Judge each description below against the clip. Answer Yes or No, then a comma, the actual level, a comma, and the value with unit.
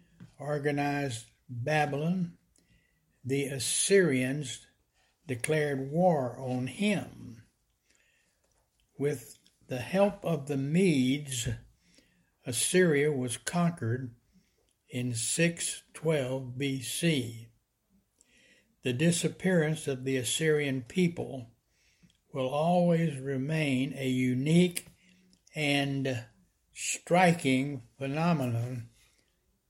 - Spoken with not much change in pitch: No, average, 4.5 semitones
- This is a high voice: No, medium, 140 Hz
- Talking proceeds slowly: Yes, slow, 70 wpm